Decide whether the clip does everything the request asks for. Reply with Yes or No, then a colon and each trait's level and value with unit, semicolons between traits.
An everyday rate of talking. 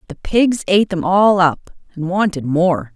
Yes: average, 185 wpm